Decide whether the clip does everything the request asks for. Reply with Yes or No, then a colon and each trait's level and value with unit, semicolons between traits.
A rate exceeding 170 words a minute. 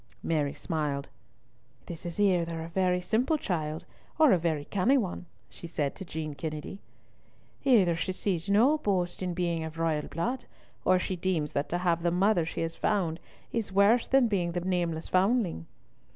Yes: average, 180 wpm